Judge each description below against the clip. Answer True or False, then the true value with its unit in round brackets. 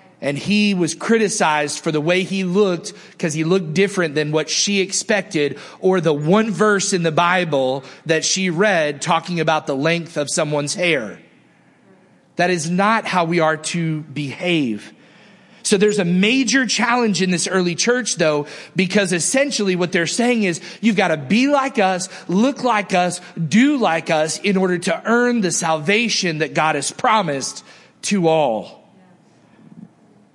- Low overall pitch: False (180 Hz)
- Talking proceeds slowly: False (160 wpm)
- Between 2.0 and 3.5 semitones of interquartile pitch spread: False (4.5 semitones)